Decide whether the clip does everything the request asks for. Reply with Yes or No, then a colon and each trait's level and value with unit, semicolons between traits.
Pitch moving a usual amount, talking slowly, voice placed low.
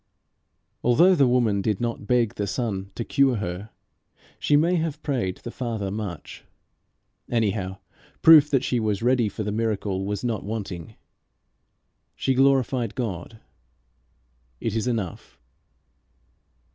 Yes: average, 4.1 semitones; slow, 130 wpm; low, 115 Hz